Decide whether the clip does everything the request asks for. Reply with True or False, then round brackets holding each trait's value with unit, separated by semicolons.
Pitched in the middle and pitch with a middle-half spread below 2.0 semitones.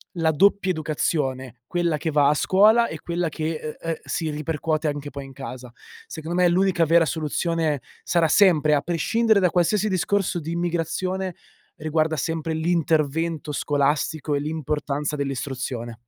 False (160 Hz; 2.8 semitones)